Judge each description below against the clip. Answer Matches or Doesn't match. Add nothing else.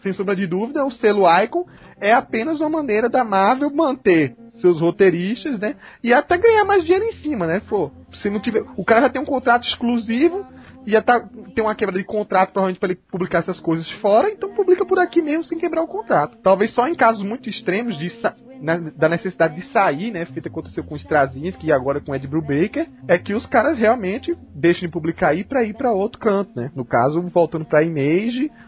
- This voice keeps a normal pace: Doesn't match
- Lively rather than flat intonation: Matches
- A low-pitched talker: Doesn't match